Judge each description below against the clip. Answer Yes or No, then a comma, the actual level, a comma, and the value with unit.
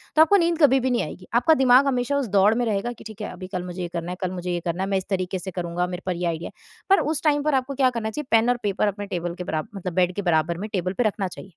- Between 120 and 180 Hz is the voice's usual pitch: No, high, 195 Hz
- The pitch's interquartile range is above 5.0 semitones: Yes, wide, 5.6 semitones